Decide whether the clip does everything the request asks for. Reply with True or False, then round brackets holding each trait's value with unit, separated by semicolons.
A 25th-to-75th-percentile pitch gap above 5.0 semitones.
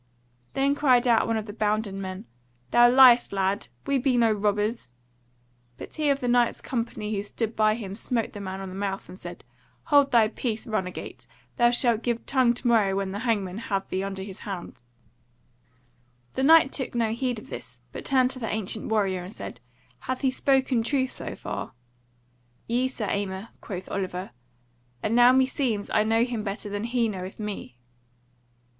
False (3.7 semitones)